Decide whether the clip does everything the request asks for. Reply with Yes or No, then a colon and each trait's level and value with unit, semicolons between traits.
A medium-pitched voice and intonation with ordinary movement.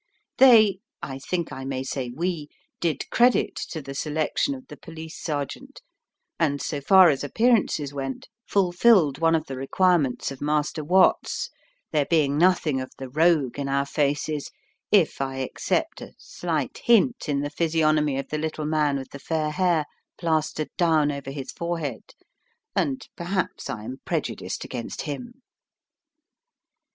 Yes: medium, 155 Hz; average, 3.9 semitones